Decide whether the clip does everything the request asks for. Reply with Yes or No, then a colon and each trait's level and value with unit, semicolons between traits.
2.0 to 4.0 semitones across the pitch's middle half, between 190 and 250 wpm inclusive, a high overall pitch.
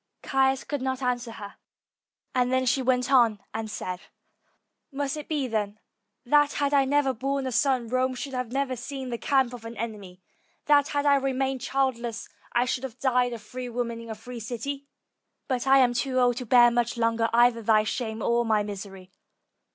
Yes: average, 2.7 semitones; average, 195 wpm; very high, 250 Hz